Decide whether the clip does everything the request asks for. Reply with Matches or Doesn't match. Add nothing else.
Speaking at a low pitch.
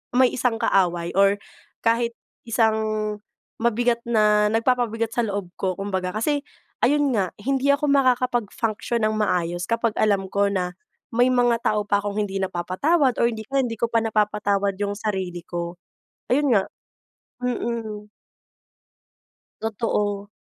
Doesn't match